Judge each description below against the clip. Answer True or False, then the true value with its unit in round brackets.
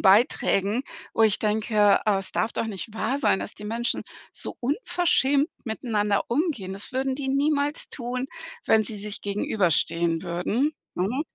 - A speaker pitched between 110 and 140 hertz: False (220 Hz)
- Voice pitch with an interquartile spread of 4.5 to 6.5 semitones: True (4.8 semitones)